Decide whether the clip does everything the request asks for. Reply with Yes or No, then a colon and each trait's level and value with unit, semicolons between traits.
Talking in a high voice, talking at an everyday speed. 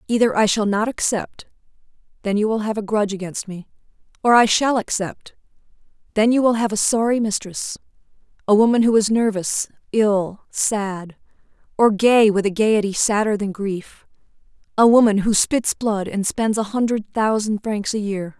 Yes: high, 210 Hz; average, 170 wpm